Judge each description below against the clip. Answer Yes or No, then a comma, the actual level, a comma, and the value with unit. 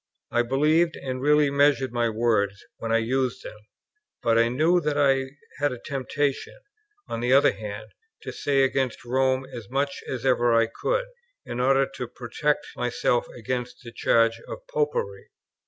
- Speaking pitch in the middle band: No, low, 130 Hz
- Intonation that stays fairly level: No, average, 3.2 semitones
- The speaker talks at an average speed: Yes, average, 165 wpm